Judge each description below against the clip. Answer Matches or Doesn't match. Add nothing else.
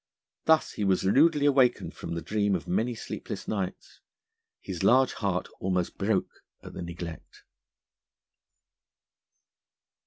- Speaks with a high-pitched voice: Doesn't match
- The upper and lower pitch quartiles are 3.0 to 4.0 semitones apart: Doesn't match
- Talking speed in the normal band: Doesn't match